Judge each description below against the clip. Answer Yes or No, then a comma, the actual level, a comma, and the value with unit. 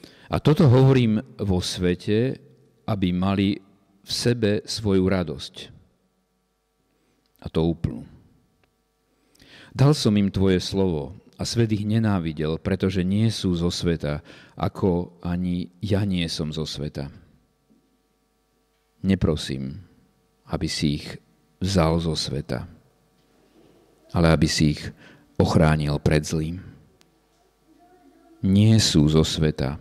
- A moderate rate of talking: No, slow, 105 wpm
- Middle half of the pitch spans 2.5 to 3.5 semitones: No, average, 5.0 semitones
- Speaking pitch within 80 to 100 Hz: Yes, very low, 90 Hz